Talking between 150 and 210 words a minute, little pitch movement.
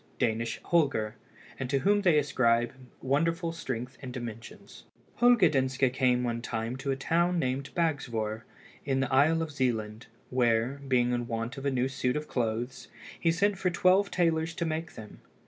No: average, 170 wpm; average, 5.3 semitones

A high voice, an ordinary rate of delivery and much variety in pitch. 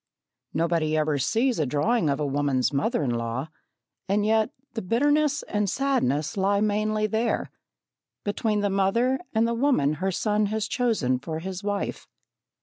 Yes: high, 205 Hz; average, 155 wpm; wide, 6.6 semitones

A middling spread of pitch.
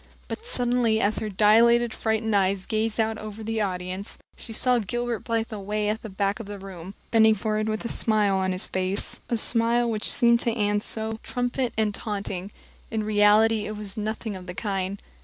No: narrow, 2.1 semitones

